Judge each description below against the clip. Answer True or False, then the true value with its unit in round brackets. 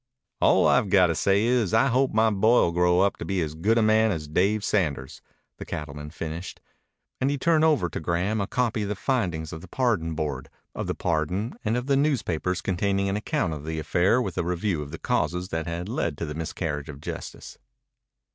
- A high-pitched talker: False (95 Hz)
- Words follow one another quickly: True (220 wpm)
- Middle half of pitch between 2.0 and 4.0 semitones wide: False (5.5 semitones)